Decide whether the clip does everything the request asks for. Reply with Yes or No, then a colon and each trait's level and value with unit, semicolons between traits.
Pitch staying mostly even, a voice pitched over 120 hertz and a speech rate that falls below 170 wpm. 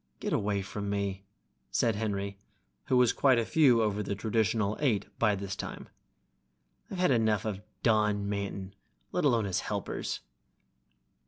No: narrow, 2.3 semitones; low, 105 Hz; average, 150 wpm